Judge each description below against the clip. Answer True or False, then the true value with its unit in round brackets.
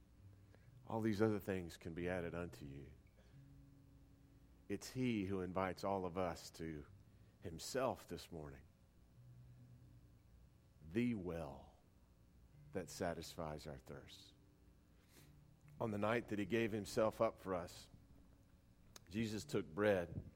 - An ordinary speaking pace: False (115 wpm)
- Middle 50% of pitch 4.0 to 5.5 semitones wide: True (4.3 semitones)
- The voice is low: True (95 Hz)